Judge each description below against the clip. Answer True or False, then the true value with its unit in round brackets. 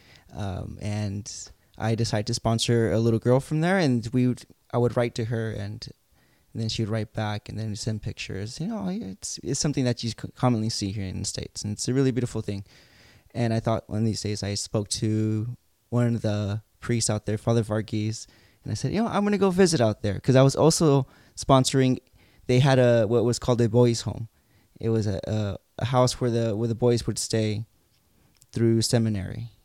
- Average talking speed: False (220 wpm)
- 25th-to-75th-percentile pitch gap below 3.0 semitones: True (2.6 semitones)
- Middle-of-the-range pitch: False (115 Hz)